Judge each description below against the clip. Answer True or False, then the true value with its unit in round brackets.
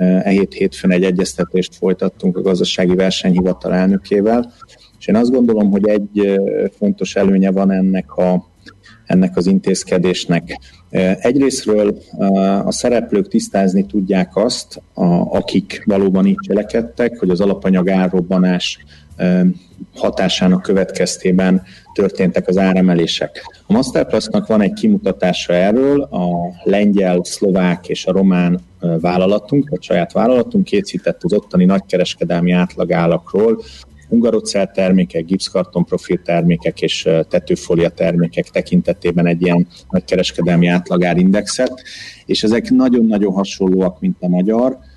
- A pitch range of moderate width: False (2.2 semitones)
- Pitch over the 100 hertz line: False (95 Hz)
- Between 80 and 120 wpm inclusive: True (115 wpm)